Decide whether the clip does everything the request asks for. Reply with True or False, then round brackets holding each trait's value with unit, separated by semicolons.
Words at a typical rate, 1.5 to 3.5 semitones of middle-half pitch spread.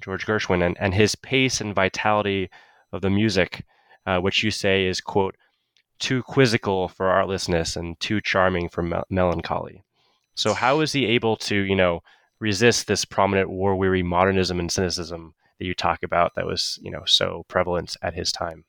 True (180 wpm; 2.9 semitones)